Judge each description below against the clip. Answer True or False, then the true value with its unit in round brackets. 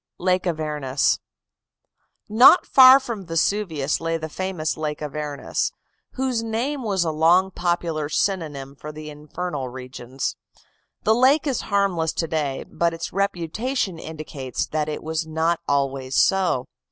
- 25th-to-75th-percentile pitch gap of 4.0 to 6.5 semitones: True (4.5 semitones)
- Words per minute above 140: False (135 wpm)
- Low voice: False (165 Hz)